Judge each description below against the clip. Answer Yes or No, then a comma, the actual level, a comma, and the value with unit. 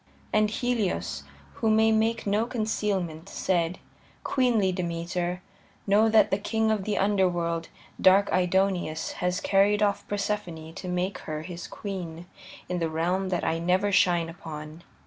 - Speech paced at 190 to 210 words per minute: No, average, 145 wpm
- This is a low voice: No, medium, 185 Hz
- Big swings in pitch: No, average, 3.5 semitones